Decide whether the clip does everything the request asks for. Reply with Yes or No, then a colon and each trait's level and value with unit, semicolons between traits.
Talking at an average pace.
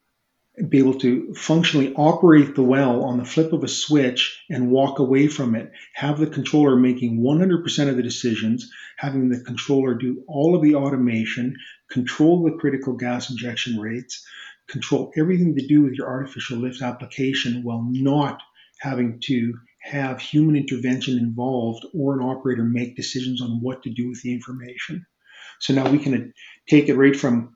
Yes: average, 170 wpm